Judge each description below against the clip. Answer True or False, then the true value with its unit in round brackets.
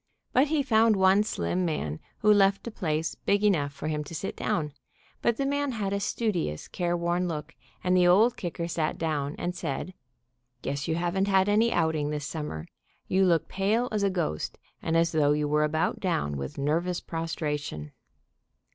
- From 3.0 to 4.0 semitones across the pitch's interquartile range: False (4.7 semitones)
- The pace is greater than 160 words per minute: True (180 wpm)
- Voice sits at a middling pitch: True (175 Hz)